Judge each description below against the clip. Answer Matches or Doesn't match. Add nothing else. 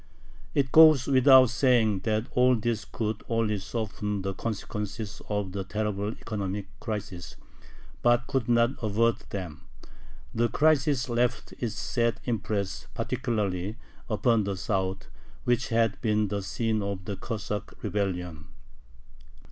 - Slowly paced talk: Matches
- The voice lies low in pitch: Matches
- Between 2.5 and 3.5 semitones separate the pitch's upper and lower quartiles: Matches